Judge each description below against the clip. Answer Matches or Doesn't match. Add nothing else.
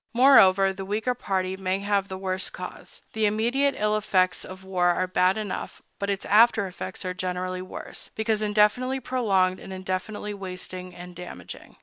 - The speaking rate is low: Doesn't match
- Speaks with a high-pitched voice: Matches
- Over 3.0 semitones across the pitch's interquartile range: Doesn't match